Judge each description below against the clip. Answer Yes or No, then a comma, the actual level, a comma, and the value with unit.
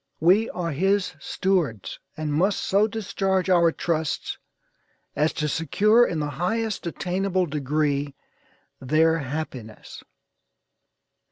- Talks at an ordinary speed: No, slow, 105 wpm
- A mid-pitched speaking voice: Yes, medium, 165 Hz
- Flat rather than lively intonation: No, average, 4.4 semitones